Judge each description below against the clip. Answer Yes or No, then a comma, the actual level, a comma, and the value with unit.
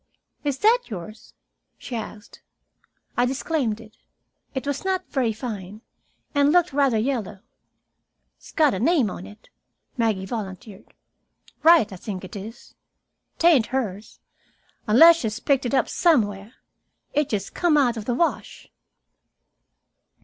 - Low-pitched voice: No, high, 240 Hz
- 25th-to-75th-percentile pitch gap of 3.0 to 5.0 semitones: No, wide, 5.4 semitones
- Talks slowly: Yes, slow, 130 wpm